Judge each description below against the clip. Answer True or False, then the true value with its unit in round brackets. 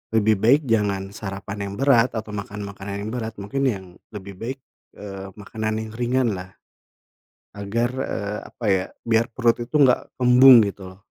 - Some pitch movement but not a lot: True (3.1 semitones)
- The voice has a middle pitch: False (110 Hz)